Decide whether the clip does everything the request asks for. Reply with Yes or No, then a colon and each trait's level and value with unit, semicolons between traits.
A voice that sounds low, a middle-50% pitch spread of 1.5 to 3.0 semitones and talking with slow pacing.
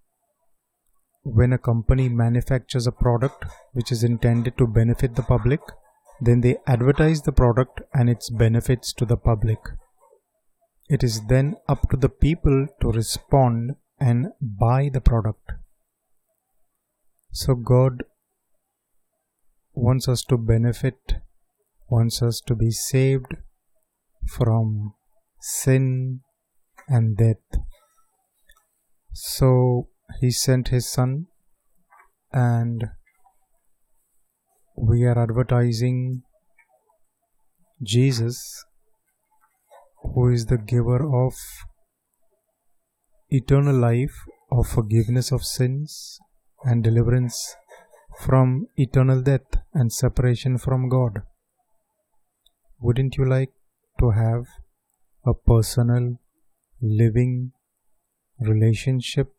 Yes: low, 125 Hz; narrow, 2.4 semitones; slow, 90 wpm